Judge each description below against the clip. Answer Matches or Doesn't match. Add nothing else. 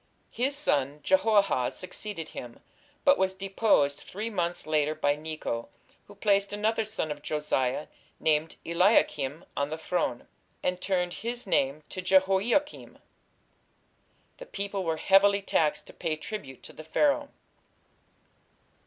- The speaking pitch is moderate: Matches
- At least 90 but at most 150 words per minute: Matches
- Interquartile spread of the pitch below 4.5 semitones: Doesn't match